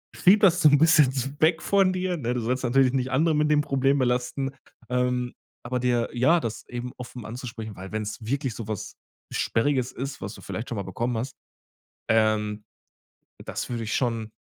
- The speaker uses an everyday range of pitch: Yes, average, 3.5 semitones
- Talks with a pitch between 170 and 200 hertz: No, low, 125 Hz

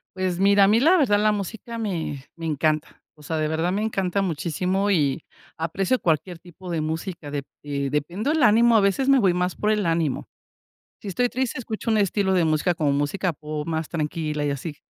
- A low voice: No, medium, 180 Hz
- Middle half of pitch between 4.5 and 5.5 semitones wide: Yes, average, 4.9 semitones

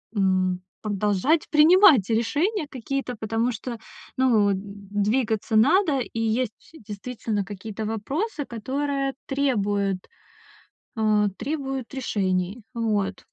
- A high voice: Yes, high, 225 Hz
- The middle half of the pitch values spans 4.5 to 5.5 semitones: Yes, average, 4.8 semitones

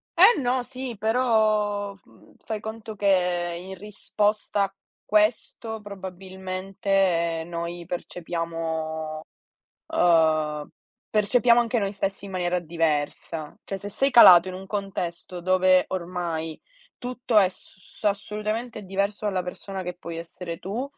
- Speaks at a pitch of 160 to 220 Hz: Yes, high, 190 Hz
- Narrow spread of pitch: No, average, 3.5 semitones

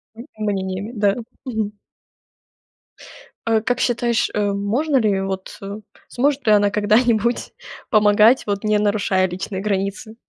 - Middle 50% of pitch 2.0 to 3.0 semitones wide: Yes, narrow, 2.6 semitones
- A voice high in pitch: Yes, high, 210 Hz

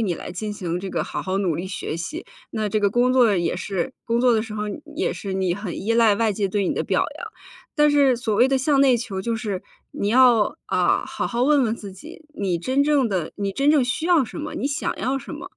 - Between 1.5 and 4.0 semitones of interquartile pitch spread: No, average, 5.2 semitones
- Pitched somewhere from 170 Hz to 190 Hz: No, high, 225 Hz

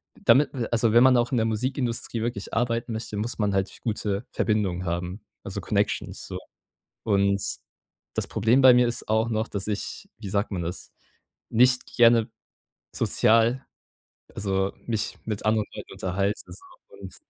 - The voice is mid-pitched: No, low, 110 Hz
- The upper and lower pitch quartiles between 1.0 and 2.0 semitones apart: No, average, 2.9 semitones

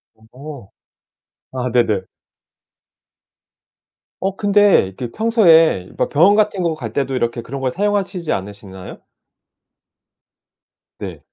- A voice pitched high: No, medium, 140 Hz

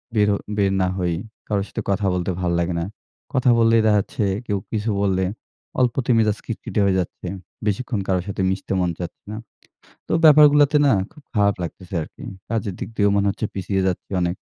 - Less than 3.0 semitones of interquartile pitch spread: No, average, 3.3 semitones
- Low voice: Yes, low, 100 Hz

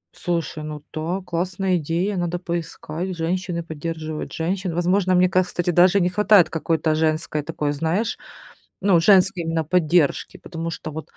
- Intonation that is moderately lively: No, narrow, 2.3 semitones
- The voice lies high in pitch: No, medium, 170 Hz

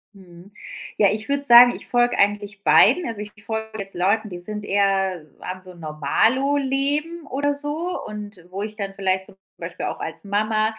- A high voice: Yes, high, 210 Hz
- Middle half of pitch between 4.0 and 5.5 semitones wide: Yes, average, 4.9 semitones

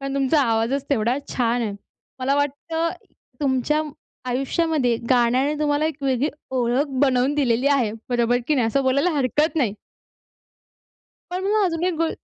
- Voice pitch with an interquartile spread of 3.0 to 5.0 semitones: Yes, average, 3.5 semitones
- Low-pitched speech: No, very high, 275 Hz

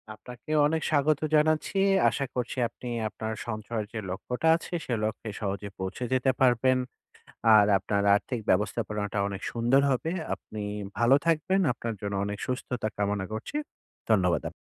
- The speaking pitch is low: Yes, low, 115 Hz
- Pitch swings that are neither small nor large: Yes, average, 4.3 semitones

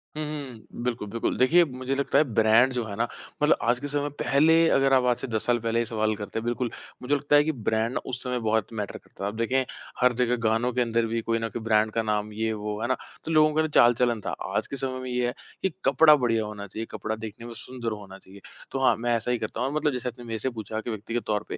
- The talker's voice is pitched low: Yes, low, 120 Hz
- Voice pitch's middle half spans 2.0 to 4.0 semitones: Yes, average, 2.8 semitones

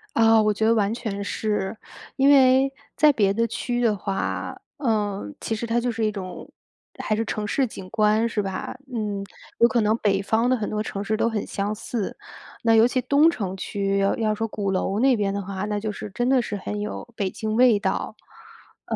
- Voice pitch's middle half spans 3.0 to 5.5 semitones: No, narrow, 2.6 semitones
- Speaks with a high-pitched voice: Yes, high, 215 Hz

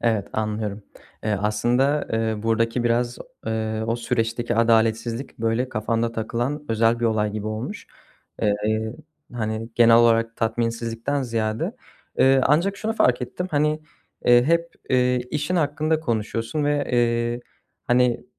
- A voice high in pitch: No, low, 115 Hz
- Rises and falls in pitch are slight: Yes, narrow, 2.3 semitones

